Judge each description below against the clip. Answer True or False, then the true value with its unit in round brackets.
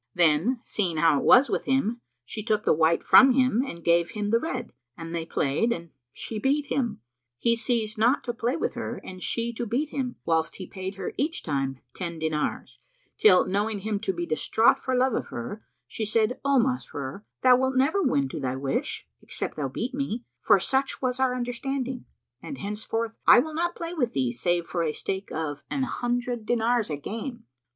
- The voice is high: True (225 Hz)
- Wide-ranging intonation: True (7.0 semitones)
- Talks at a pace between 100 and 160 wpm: False (200 wpm)